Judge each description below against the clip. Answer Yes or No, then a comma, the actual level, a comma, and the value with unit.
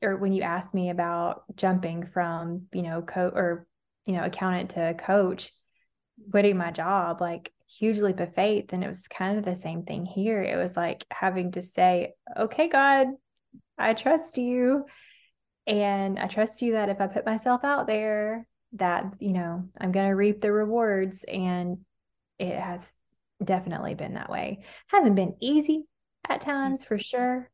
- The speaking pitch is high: Yes, high, 195 Hz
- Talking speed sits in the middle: Yes, average, 170 wpm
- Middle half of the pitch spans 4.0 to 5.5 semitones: No, average, 3.5 semitones